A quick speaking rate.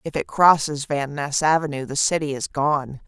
No: average, 195 wpm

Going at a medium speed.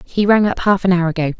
No: fast, 300 wpm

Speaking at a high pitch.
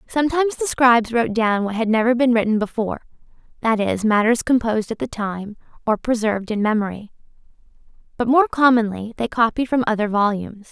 Yes: high, 230 Hz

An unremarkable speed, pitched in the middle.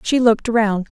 No: average, 185 wpm; high, 220 Hz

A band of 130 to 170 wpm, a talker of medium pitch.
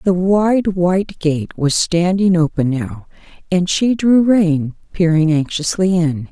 Yes: average, 145 wpm; medium, 175 Hz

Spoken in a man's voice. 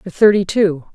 No: female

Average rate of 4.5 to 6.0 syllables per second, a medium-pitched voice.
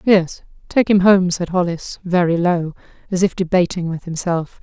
Yes: 4.6 syllables/s; medium, 180 Hz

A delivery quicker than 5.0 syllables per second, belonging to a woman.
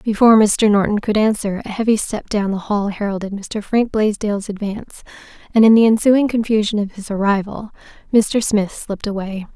Yes: 5.3 syllables/s; female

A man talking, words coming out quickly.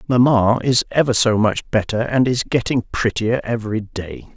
No: male; average, 165 wpm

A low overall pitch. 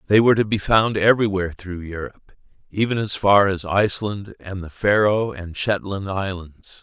Yes: low, 100 Hz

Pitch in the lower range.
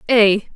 No: high, 215 Hz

